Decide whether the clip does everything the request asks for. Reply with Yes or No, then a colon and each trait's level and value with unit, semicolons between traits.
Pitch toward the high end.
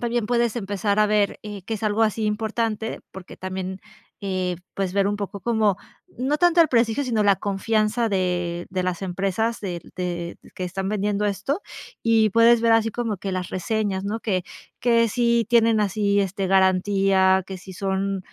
Yes: high, 205 Hz